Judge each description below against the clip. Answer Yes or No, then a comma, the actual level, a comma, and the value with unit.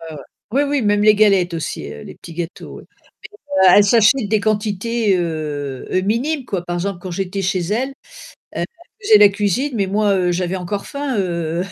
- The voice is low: No, high, 200 Hz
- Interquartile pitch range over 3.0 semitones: Yes, average, 3.7 semitones